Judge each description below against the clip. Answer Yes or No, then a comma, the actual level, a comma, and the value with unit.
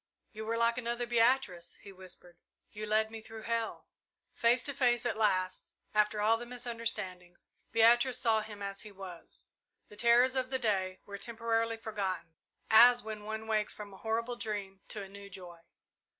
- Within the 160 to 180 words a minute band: Yes, average, 175 wpm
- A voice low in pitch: No, high, 220 Hz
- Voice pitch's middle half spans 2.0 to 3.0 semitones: Yes, average, 2.7 semitones